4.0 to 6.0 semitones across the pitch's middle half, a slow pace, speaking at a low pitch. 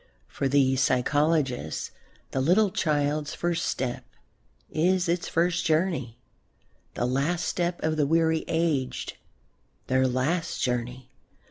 No: average, 4.4 semitones; slow, 115 wpm; medium, 150 Hz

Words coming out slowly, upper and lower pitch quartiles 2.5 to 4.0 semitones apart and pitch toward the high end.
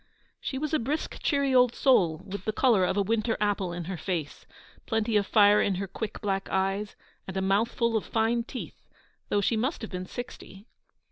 No: average, 200 wpm; average, 3.5 semitones; high, 210 Hz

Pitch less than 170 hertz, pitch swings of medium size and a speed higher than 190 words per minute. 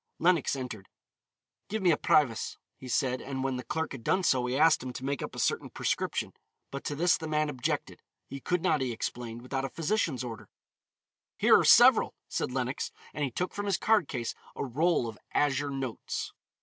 Yes: low, 135 Hz; average, 4.1 semitones; average, 200 wpm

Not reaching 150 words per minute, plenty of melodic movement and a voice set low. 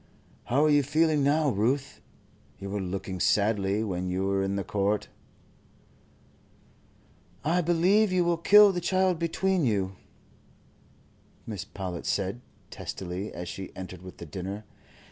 Yes: average, 140 wpm; wide, 9.0 semitones; low, 105 Hz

